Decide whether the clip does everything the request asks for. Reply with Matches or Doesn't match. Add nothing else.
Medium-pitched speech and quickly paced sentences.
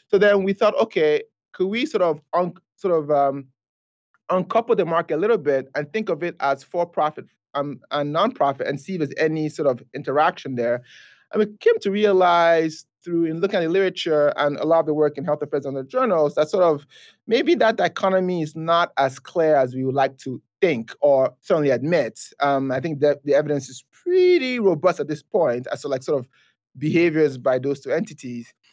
Matches